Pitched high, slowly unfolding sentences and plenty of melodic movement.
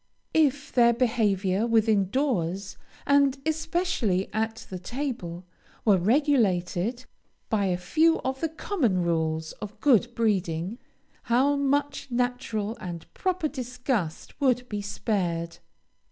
Yes: high, 225 Hz; slow, 115 wpm; wide, 6.3 semitones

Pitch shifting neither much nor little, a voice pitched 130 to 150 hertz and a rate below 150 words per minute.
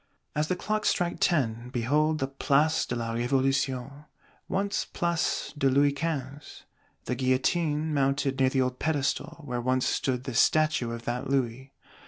No: average, 3.2 semitones; low, 135 Hz; average, 155 wpm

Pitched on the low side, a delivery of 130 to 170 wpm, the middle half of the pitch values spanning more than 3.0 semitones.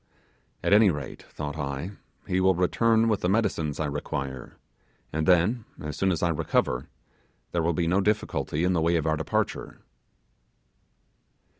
Yes: very low, 85 Hz; average, 160 wpm; average, 4.0 semitones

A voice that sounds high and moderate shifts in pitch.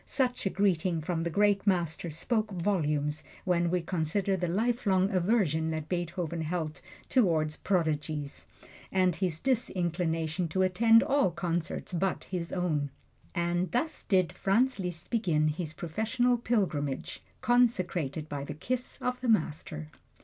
No: medium, 180 Hz; average, 4.2 semitones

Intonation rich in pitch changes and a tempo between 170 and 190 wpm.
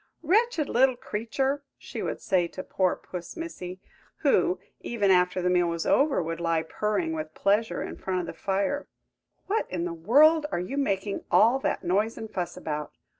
Yes: wide, 7.2 semitones; average, 180 wpm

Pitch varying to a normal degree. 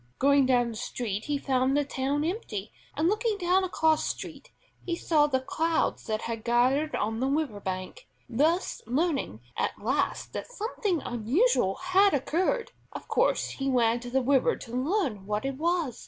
No: wide, 6.0 semitones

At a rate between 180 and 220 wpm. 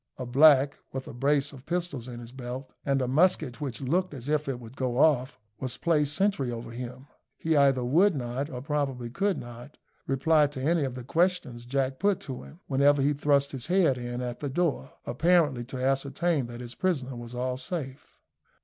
Yes: average, 200 wpm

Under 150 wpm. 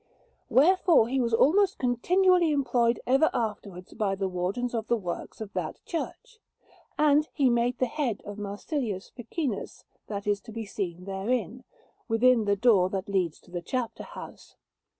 No: average, 155 wpm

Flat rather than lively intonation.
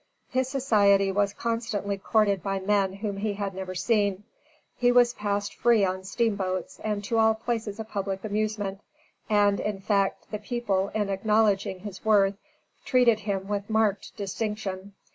Yes: narrow, 1.9 semitones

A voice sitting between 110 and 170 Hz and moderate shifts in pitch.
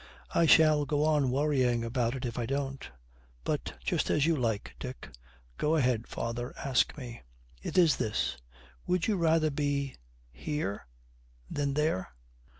Yes: medium, 140 Hz; average, 3.9 semitones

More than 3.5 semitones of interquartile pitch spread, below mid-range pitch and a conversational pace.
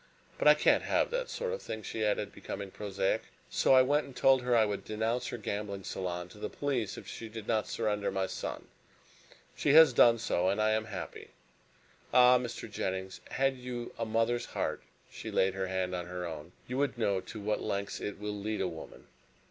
No: average, 4.0 semitones; low, 110 Hz; fast, 210 wpm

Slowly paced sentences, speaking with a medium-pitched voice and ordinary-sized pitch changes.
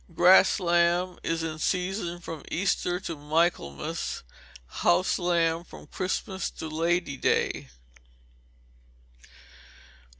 No: slow, 95 wpm; medium, 175 Hz; narrow, 1.7 semitones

